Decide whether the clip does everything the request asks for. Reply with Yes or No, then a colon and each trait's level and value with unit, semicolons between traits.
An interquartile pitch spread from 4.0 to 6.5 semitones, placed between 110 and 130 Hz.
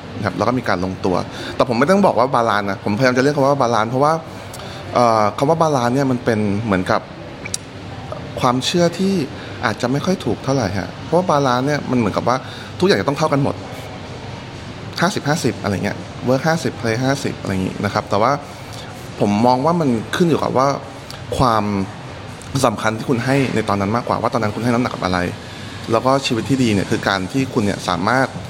Yes: average, 4.5 semitones; low, 120 Hz